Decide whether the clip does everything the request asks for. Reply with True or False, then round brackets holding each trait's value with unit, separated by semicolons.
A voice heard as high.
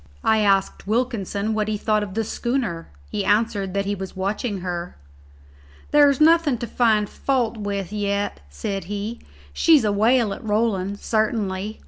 True (210 Hz)